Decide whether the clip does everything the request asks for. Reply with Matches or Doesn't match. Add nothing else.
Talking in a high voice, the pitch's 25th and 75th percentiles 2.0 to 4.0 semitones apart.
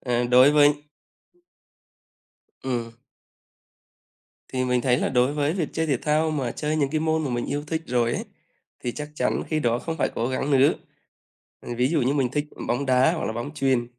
Doesn't match